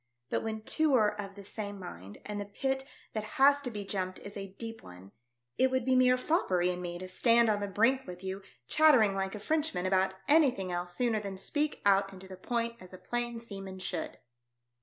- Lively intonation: No, average, 4.3 semitones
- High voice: Yes, high, 205 Hz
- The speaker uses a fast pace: Yes, fast, 220 wpm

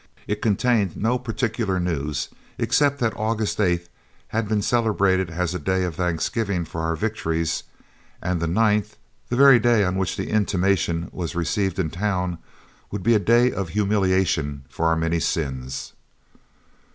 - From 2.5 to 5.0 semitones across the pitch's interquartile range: Yes, average, 4.4 semitones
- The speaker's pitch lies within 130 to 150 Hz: No, very low, 95 Hz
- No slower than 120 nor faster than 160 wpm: Yes, average, 155 wpm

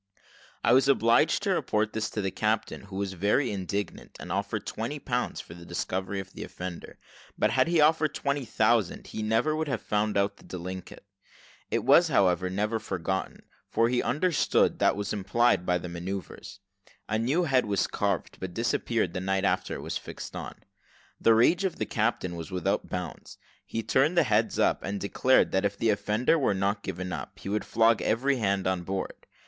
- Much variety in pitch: No, average, 3.9 semitones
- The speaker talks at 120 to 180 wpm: No, average, 195 wpm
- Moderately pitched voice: No, low, 105 Hz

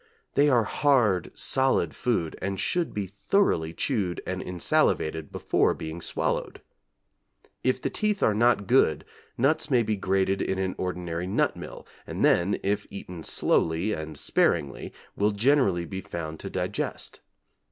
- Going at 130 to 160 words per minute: Yes, average, 145 wpm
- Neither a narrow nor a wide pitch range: No, wide, 5.9 semitones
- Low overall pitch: Yes, very low, 95 Hz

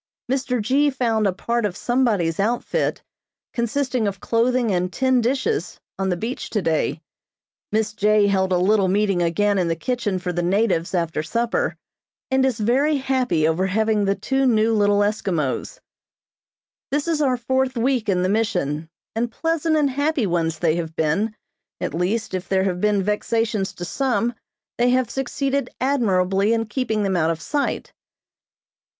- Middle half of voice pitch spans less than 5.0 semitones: No, wide, 5.4 semitones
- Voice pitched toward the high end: Yes, high, 215 Hz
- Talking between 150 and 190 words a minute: Yes, average, 165 wpm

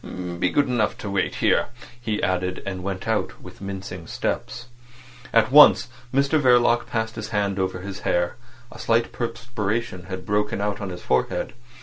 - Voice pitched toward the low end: Yes, low, 105 Hz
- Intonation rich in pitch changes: No, average, 4.0 semitones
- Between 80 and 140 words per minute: No, average, 165 wpm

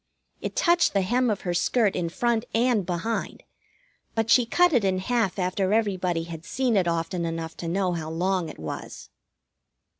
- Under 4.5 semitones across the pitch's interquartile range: No, average, 5.1 semitones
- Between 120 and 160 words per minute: No, average, 180 wpm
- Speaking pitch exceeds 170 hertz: Yes, high, 190 Hz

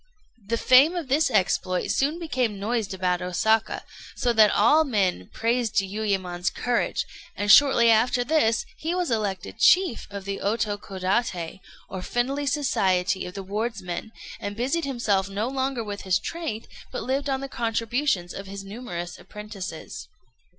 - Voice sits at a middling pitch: No, high, 220 Hz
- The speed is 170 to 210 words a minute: No, average, 150 wpm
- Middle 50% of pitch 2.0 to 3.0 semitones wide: No, average, 4.7 semitones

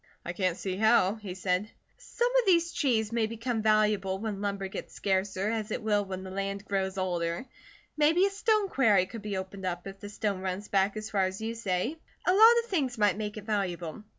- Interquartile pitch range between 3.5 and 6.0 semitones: No, average, 3.1 semitones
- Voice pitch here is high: Yes, high, 205 Hz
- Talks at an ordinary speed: No, fast, 215 wpm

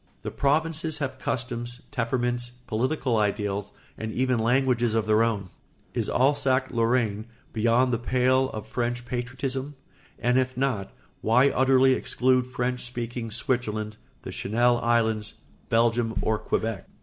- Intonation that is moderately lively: No, narrow, 2.3 semitones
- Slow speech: Yes, slow, 130 wpm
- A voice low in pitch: Yes, low, 120 Hz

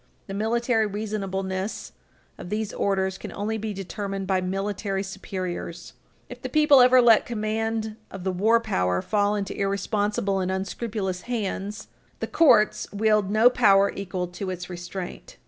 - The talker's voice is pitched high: Yes, high, 200 Hz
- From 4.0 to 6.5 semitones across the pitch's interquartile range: No, narrow, 2.5 semitones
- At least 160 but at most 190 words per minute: No, average, 145 wpm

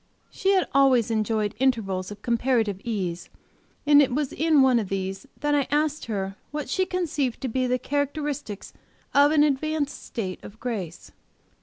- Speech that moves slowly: No, average, 165 wpm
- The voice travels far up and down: Yes, wide, 5.8 semitones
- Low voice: No, very high, 255 Hz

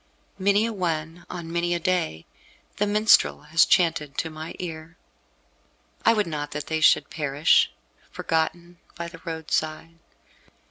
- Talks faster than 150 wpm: No, average, 140 wpm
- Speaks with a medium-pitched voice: Yes, medium, 165 Hz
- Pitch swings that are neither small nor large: No, narrow, 2.0 semitones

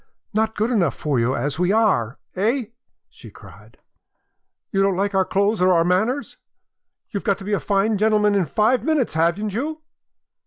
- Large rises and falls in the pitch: No, average, 3.4 semitones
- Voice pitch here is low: No, high, 200 Hz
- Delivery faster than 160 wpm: Yes, average, 180 wpm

